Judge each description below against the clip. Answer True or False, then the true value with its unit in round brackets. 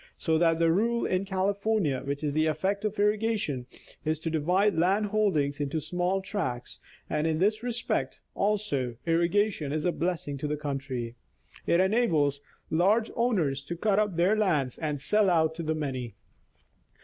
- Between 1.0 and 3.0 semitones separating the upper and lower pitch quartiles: False (5.6 semitones)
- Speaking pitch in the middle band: True (170 Hz)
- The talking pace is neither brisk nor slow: True (165 wpm)